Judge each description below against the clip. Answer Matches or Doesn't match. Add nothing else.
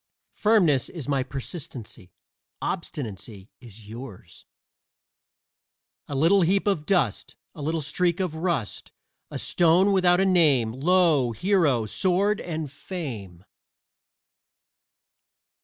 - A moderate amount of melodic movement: Doesn't match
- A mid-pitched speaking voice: Matches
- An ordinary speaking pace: Doesn't match